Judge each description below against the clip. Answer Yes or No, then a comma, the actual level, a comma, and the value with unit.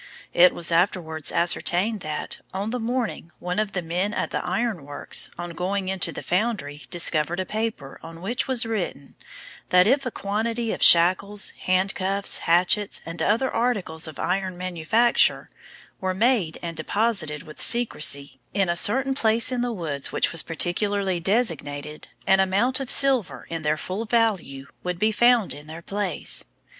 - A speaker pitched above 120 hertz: Yes, high, 190 Hz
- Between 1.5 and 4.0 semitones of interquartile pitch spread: No, average, 5.0 semitones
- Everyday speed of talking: Yes, average, 165 wpm